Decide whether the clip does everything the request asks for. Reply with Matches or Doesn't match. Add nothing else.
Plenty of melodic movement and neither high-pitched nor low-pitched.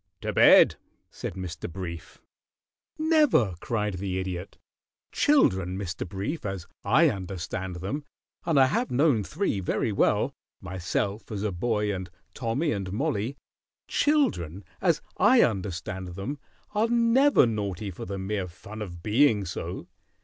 Doesn't match